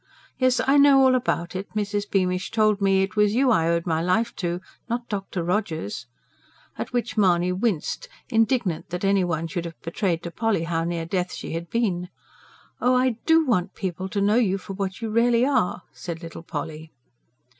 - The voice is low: No, high, 195 Hz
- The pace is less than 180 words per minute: No, average, 190 wpm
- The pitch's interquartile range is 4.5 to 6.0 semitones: Yes, average, 4.9 semitones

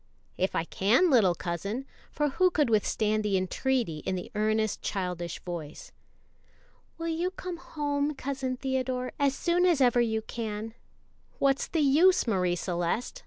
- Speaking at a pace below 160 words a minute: Yes, average, 150 wpm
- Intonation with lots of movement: Yes, wide, 6.7 semitones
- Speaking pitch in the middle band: No, high, 240 Hz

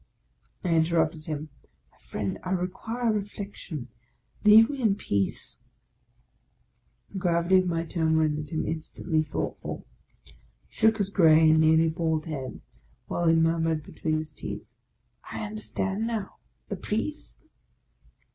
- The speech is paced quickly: No, average, 145 wpm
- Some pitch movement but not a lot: Yes, average, 4.1 semitones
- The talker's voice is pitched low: No, medium, 165 Hz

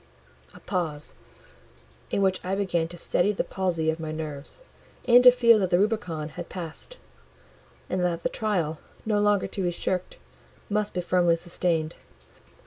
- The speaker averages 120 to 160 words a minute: Yes, average, 155 wpm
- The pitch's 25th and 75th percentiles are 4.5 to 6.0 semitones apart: No, average, 3.9 semitones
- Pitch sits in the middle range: Yes, medium, 180 Hz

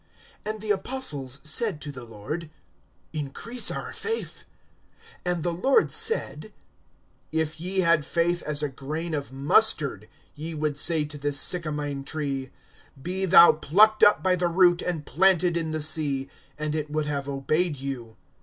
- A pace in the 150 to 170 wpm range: Yes, average, 155 wpm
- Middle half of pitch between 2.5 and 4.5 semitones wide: Yes, average, 3.7 semitones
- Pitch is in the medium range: Yes, medium, 155 Hz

